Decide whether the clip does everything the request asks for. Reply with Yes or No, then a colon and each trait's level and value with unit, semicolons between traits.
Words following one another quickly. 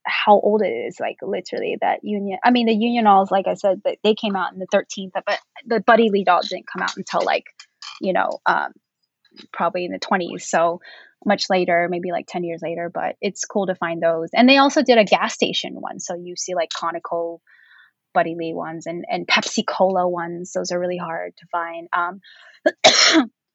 Yes: fast, 210 wpm